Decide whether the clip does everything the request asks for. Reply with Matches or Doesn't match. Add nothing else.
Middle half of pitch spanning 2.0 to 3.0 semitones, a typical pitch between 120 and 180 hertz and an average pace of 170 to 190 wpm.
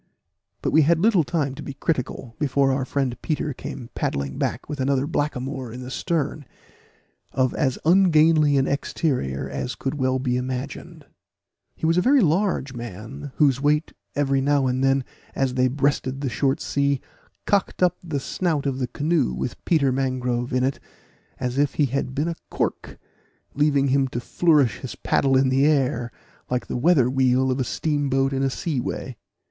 Matches